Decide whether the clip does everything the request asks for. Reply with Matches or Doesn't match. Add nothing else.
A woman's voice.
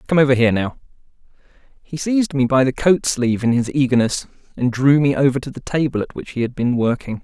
Doesn't match